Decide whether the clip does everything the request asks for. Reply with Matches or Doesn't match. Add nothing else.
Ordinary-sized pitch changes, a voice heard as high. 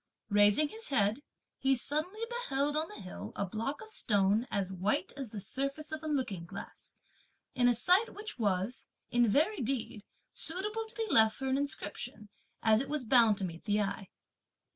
Doesn't match